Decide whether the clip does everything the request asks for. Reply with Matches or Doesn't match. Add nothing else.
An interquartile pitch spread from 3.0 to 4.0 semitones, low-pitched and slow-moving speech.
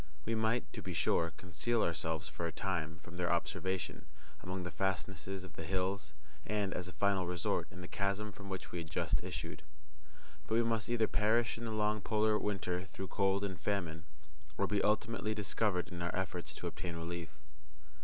Doesn't match